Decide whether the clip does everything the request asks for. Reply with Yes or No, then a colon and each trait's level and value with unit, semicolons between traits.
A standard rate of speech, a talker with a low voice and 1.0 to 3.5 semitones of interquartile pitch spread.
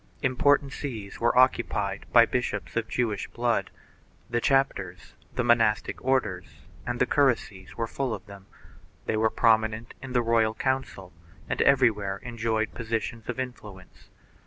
Yes: average, 145 wpm; low, 115 Hz; average, 2.9 semitones